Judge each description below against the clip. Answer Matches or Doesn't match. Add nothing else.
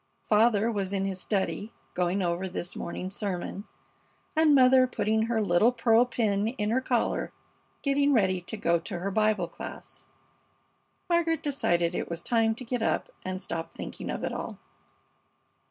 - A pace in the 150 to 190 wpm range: Matches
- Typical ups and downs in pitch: Matches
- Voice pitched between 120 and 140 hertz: Doesn't match